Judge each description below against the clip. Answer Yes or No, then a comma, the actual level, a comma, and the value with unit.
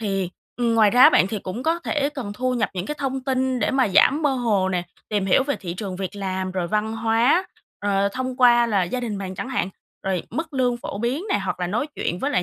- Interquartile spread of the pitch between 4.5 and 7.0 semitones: Yes, average, 5.0 semitones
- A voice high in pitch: Yes, high, 225 Hz